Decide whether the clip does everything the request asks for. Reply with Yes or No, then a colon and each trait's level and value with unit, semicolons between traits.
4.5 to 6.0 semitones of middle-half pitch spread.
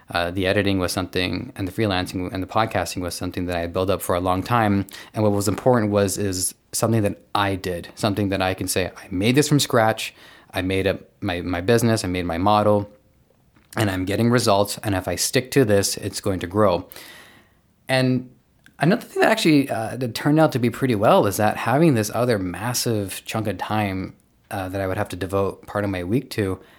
No: average, 3.5 semitones